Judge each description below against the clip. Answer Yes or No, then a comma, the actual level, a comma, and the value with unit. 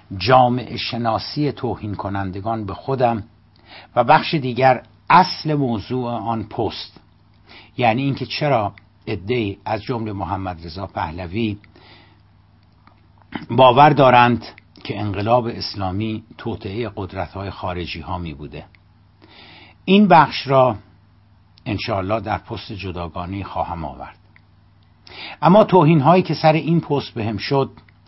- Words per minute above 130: No, average, 110 wpm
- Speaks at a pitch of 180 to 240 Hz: No, low, 110 Hz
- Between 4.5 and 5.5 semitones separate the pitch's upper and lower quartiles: No, average, 4.0 semitones